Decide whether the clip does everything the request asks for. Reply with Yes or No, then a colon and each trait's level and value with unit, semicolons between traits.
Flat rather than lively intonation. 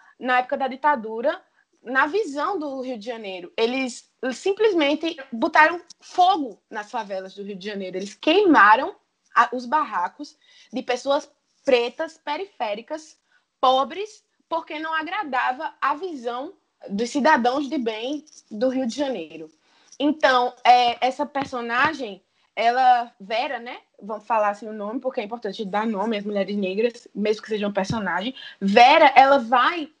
No: average, 5.3 semitones